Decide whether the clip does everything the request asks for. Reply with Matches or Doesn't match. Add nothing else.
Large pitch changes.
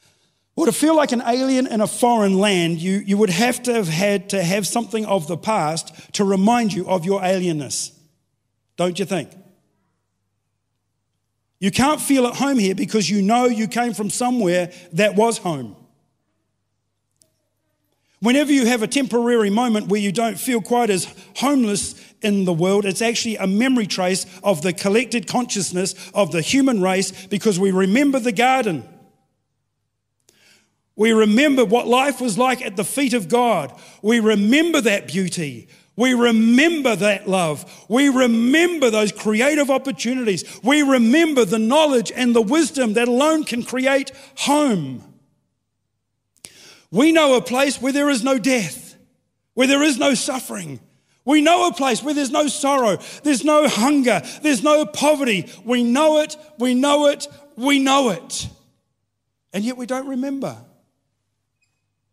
Matches